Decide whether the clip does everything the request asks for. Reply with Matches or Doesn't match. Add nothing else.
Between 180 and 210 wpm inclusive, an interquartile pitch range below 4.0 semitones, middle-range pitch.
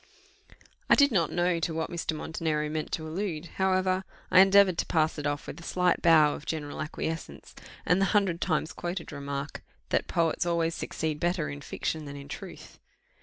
Matches